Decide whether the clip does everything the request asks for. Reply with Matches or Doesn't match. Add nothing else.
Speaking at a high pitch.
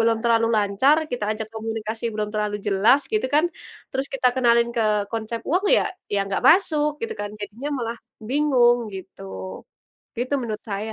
Matches